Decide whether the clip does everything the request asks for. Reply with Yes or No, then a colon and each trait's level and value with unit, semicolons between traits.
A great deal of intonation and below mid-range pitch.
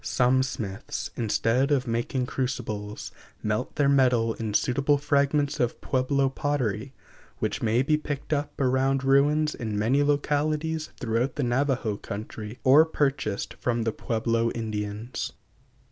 No: average, 3.8 semitones; low, 130 Hz